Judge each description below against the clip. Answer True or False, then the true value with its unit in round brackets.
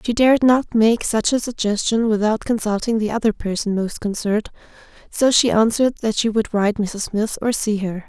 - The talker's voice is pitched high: True (220 Hz)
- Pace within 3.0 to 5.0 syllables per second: False (5.3 syllables/s)